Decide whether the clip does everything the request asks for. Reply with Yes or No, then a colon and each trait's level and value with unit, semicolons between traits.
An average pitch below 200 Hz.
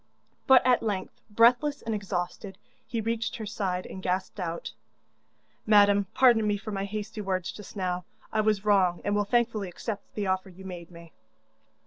No: high, 205 Hz